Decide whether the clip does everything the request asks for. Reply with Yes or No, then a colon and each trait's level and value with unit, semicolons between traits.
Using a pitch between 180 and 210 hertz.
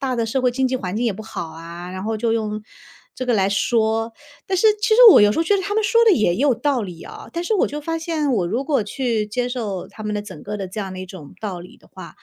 No: high, 225 Hz